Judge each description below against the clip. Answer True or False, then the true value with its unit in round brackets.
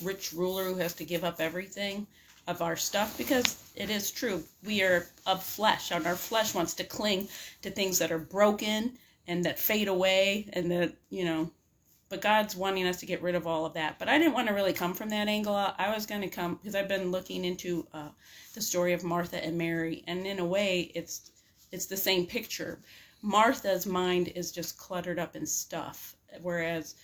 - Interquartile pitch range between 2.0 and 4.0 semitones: True (2.7 semitones)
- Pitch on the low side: False (185 Hz)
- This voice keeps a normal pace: False (210 wpm)